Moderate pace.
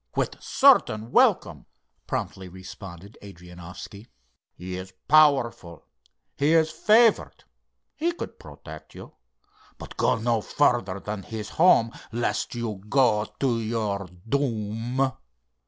No: slow, 110 wpm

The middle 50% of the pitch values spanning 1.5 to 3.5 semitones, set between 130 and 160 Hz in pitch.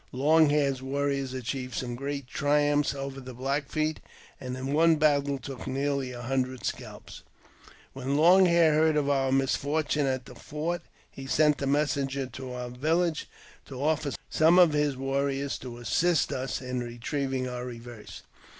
Yes: narrow, 2.4 semitones; medium, 140 Hz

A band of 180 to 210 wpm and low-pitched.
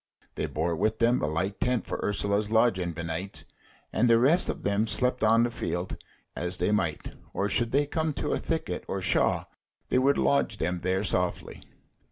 Yes: average, 190 wpm; low, 100 Hz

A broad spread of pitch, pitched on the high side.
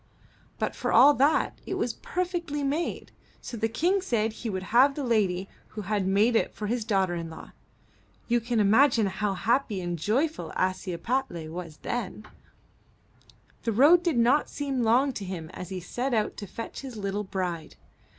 Yes: wide, 6.0 semitones; high, 220 Hz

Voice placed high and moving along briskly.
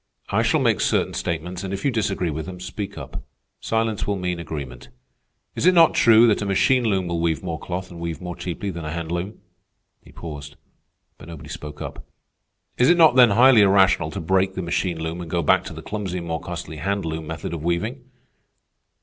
No: very low, 90 Hz; fast, 215 wpm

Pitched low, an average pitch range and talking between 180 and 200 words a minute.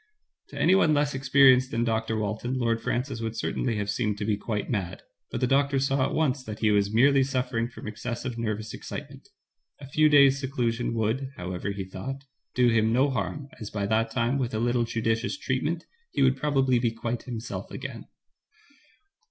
Yes: low, 120 Hz; average, 3.3 semitones; average, 185 wpm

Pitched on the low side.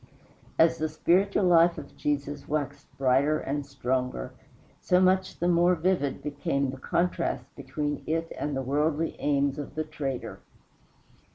No: medium, 150 Hz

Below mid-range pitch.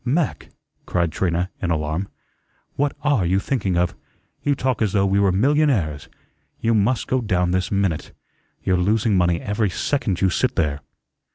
Yes: low, 100 Hz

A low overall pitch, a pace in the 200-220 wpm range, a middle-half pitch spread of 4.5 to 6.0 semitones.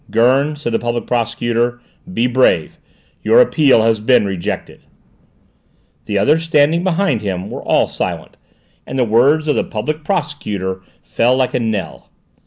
No: low, 125 Hz; average, 150 wpm; average, 5.1 semitones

